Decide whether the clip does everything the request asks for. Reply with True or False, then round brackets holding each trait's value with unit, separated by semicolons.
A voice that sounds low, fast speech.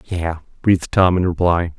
False (85 Hz; 170 wpm)